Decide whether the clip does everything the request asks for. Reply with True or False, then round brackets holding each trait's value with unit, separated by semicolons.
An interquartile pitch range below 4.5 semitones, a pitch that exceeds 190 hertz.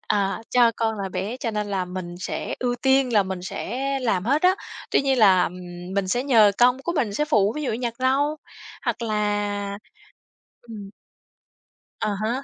True (4.1 semitones; 215 Hz)